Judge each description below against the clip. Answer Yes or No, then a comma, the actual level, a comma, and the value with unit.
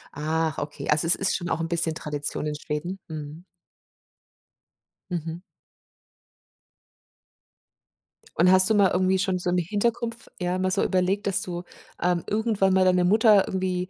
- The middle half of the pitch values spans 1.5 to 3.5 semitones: Yes, narrow, 2.6 semitones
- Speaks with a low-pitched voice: No, medium, 180 Hz